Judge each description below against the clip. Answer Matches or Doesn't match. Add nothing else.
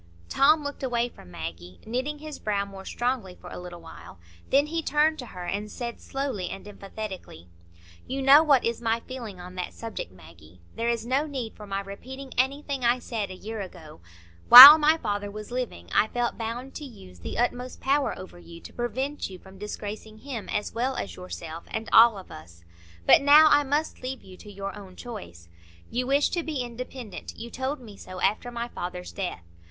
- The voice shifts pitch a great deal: Matches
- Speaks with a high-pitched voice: Matches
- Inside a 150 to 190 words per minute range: Doesn't match